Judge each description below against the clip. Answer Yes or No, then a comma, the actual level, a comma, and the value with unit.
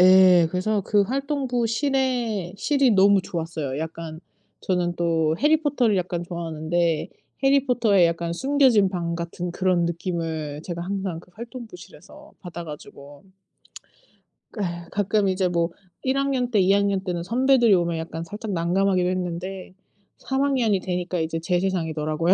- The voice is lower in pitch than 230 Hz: Yes, medium, 185 Hz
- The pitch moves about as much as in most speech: Yes, average, 4.6 semitones